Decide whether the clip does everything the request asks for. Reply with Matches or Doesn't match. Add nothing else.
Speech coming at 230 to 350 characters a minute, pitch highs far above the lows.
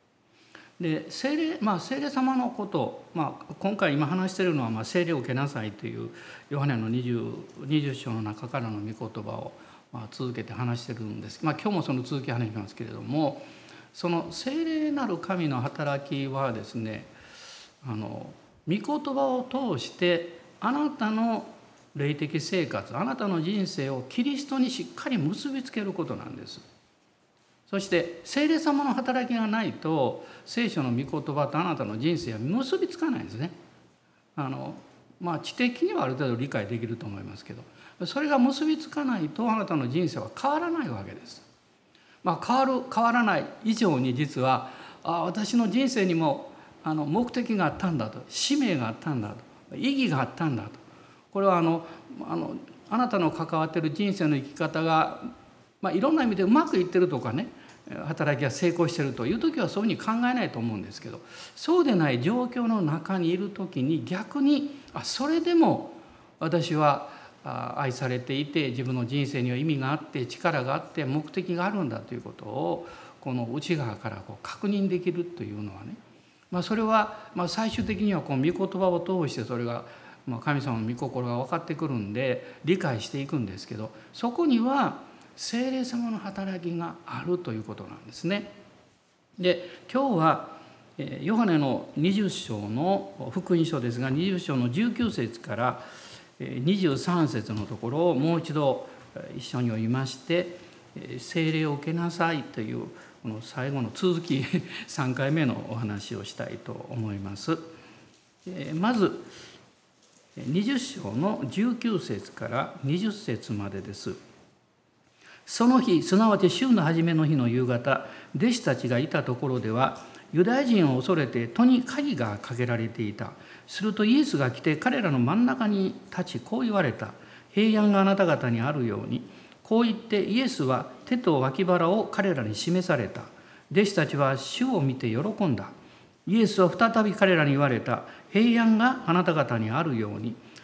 Matches